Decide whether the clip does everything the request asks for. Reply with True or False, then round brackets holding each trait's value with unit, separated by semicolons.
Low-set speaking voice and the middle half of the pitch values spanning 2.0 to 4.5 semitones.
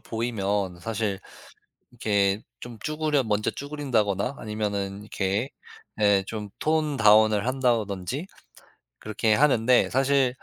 True (110 Hz; 4.2 semitones)